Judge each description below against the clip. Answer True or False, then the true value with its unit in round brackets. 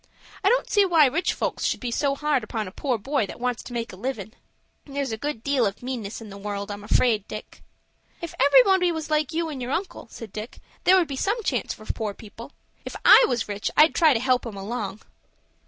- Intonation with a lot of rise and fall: True (5.8 semitones)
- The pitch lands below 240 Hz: False (250 Hz)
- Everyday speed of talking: False (230 wpm)